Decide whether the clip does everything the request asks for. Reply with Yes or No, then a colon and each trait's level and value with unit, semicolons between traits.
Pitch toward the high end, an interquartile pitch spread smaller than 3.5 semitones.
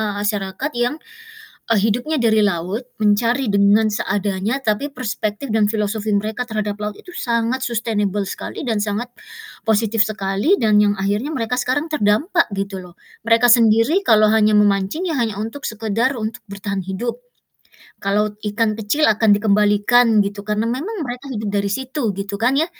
Yes: high, 215 Hz; average, 2.9 semitones